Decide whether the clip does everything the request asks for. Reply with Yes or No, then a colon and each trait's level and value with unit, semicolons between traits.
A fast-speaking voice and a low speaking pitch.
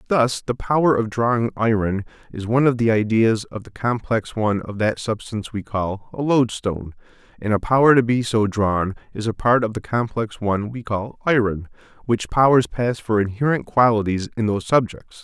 No: average, 190 wpm; low, 110 Hz